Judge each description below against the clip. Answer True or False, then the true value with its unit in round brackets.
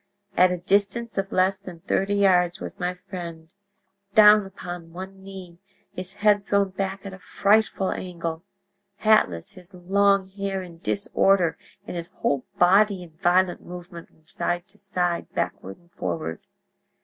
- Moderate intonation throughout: False (2.2 semitones)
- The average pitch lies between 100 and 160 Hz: False (185 Hz)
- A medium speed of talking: True (150 wpm)